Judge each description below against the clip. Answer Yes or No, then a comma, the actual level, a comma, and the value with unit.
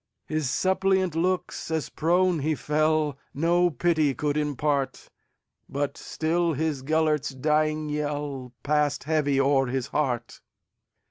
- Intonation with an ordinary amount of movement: No, narrow, 2.3 semitones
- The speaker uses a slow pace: Yes, slow, 105 wpm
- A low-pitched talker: No, medium, 150 Hz